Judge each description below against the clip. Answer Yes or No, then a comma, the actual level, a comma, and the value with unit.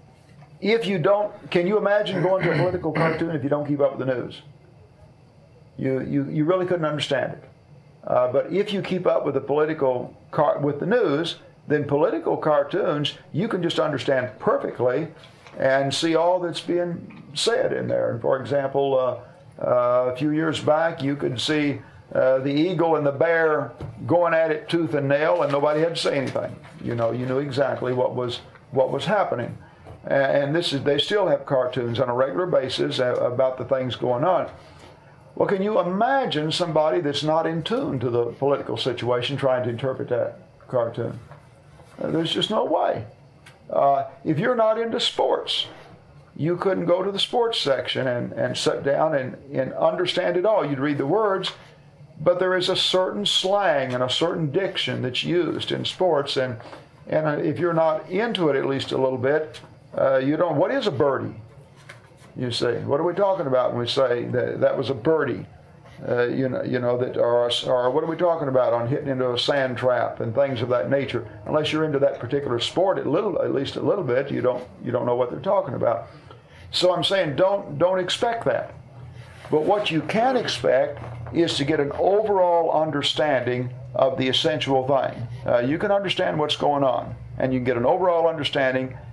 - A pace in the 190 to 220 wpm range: Yes, average, 195 wpm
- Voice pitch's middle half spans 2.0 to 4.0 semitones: No, average, 4.5 semitones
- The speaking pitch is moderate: Yes, medium, 145 Hz